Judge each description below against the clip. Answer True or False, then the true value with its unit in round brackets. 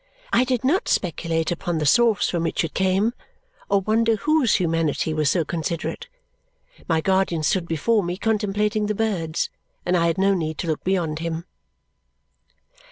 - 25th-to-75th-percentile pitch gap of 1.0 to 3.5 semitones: False (4.4 semitones)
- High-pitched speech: False (180 Hz)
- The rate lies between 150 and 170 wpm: True (165 wpm)